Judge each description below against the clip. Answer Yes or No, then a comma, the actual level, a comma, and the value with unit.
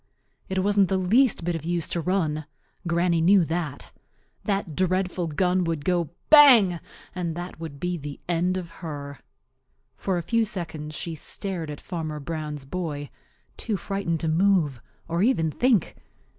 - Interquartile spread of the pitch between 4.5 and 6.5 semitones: No, average, 3.1 semitones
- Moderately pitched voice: Yes, medium, 175 Hz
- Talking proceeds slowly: No, average, 155 wpm